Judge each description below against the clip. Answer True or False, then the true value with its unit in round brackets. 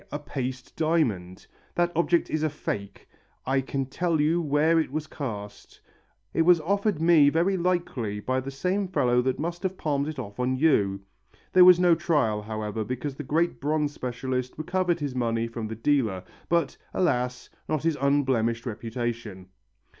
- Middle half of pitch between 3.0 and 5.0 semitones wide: False (5.5 semitones)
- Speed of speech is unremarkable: True (170 wpm)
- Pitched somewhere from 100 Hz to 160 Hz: True (140 Hz)